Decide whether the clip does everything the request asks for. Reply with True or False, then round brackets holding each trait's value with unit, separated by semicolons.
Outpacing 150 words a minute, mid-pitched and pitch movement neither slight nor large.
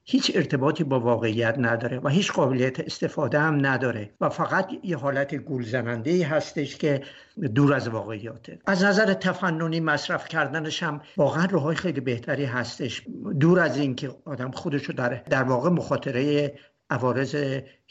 False (145 wpm; 145 Hz; 3.9 semitones)